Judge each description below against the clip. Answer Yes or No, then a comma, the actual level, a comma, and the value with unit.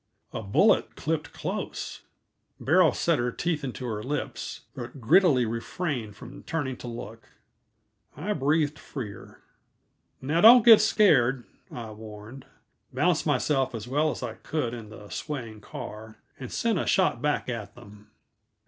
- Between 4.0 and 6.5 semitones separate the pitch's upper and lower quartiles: Yes, wide, 5.5 semitones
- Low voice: Yes, low, 130 Hz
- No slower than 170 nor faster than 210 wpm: No, average, 145 wpm